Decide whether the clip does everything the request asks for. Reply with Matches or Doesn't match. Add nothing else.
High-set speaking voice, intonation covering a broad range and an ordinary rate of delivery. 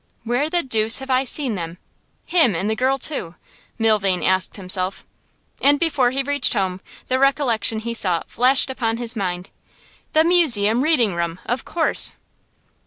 Matches